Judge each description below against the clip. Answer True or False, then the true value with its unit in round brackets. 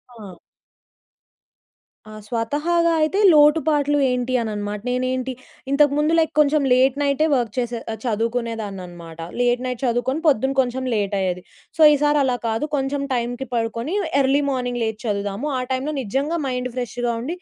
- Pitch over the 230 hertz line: True (250 Hz)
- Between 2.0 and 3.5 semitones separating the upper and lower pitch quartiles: False (4.1 semitones)